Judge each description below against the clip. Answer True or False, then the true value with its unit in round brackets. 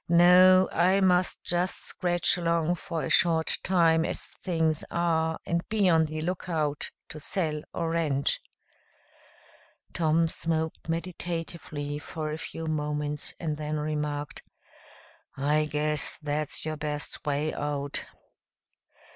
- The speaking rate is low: True (120 wpm)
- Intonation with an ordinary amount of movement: False (2.2 semitones)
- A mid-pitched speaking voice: True (160 Hz)